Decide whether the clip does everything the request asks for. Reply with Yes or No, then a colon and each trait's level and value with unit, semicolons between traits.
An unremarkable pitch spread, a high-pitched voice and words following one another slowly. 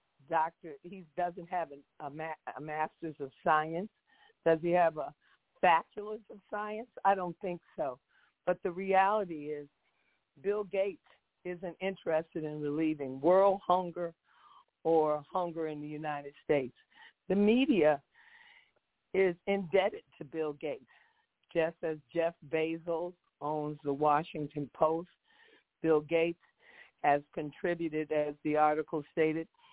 No: average, 4.0 semitones; medium, 165 Hz; slow, 125 wpm